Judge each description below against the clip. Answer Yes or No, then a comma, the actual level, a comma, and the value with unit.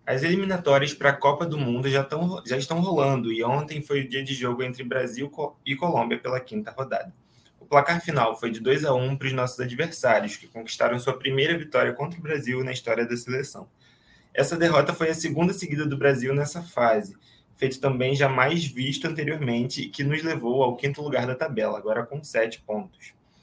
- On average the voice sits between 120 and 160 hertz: Yes, low, 135 Hz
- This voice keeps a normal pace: No, fast, 195 wpm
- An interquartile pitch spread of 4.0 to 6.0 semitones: No, average, 3.3 semitones